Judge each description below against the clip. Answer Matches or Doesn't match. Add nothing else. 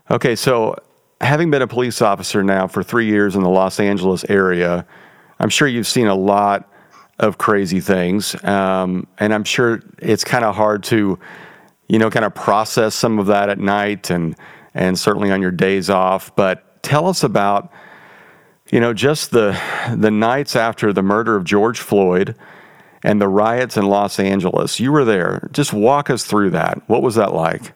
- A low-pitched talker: Matches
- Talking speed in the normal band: Matches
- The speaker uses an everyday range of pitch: Matches